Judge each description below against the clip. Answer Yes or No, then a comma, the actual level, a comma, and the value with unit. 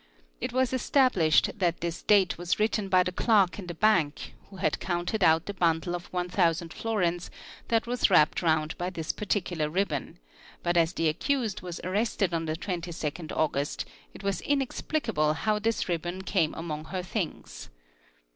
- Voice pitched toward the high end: No, medium, 180 Hz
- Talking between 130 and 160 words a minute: No, average, 175 wpm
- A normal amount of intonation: Yes, average, 3.8 semitones